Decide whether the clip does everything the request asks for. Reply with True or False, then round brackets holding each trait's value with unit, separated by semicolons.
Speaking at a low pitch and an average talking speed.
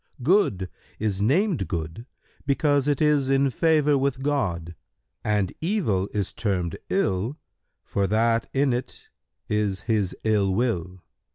False (115 Hz; 125 wpm)